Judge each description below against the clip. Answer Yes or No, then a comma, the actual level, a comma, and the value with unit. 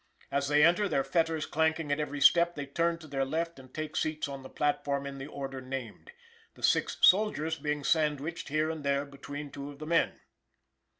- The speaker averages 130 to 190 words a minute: No, average, 200 wpm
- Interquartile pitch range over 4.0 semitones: No, narrow, 2.5 semitones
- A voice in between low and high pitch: Yes, medium, 150 Hz